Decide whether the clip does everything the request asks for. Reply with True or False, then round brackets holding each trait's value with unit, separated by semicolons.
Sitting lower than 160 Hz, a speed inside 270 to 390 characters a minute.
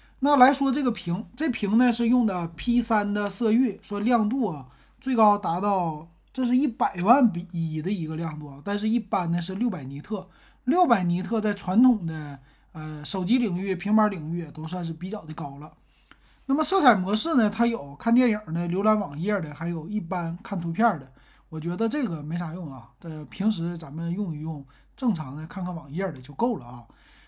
False (195 Hz; 280 characters per minute)